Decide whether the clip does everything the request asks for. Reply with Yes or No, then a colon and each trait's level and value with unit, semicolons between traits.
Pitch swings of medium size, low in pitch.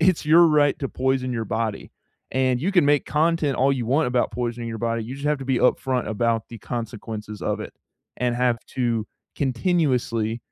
Yes: average, 3.6 semitones; low, 125 Hz